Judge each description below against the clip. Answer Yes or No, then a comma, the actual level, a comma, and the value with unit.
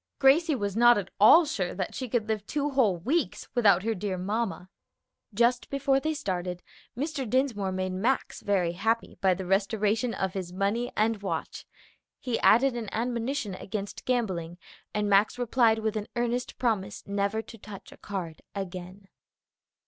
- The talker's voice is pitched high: Yes, high, 215 Hz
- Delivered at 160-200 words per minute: Yes, average, 165 wpm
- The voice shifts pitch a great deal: No, average, 4.0 semitones